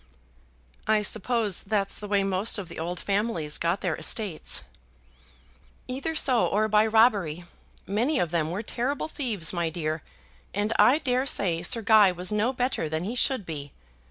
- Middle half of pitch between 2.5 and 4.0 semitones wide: No, average, 5.0 semitones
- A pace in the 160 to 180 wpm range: Yes, average, 165 wpm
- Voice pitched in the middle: No, high, 205 Hz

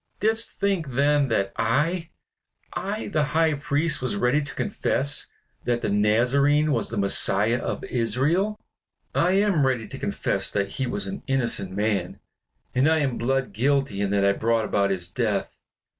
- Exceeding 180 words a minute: No, average, 165 wpm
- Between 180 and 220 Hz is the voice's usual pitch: No, low, 135 Hz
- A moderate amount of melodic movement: No, wide, 6.0 semitones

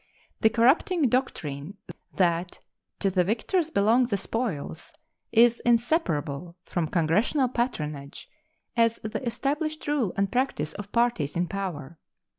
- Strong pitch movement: Yes, wide, 6.6 semitones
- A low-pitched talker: No, high, 215 Hz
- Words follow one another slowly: Yes, slow, 120 wpm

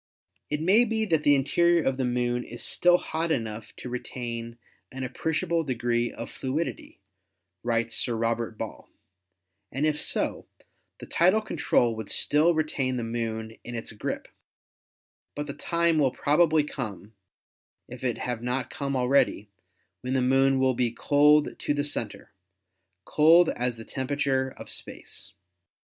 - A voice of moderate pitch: No, low, 130 Hz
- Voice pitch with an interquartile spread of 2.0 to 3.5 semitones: No, average, 4.3 semitones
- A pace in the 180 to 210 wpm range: No, average, 150 wpm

